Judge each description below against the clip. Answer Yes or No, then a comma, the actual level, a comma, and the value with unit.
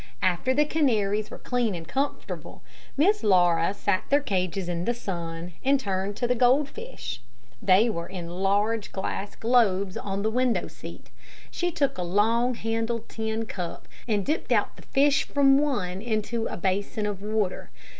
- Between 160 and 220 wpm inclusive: Yes, average, 165 wpm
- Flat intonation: No, average, 4.8 semitones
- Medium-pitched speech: No, high, 215 Hz